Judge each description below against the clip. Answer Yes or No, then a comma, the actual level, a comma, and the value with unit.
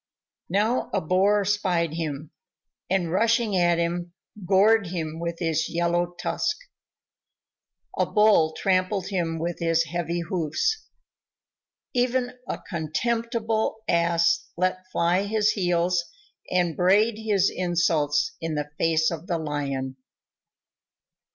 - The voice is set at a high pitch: No, medium, 175 Hz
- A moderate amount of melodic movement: Yes, average, 3.6 semitones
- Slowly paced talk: Yes, slow, 115 wpm